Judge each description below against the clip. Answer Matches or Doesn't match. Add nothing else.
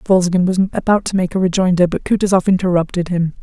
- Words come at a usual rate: Matches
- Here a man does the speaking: Doesn't match